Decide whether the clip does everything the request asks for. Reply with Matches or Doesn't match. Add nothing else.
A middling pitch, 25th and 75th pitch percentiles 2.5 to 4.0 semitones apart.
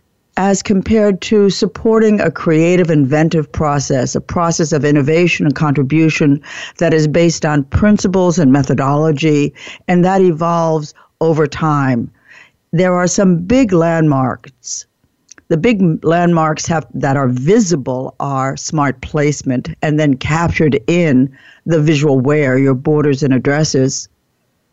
Matches